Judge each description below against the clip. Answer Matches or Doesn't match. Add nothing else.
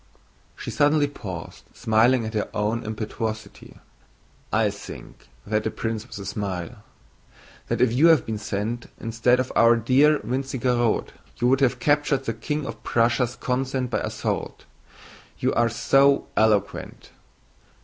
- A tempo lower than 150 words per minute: Matches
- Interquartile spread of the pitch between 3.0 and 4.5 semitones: Matches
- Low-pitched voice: Matches